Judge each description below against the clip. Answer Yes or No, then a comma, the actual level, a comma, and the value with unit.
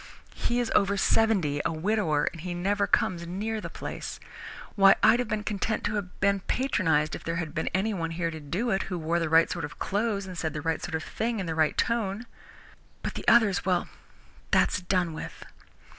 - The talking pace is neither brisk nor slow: No, fast, 210 wpm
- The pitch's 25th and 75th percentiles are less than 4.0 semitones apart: No, average, 4.3 semitones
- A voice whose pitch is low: No, medium, 185 Hz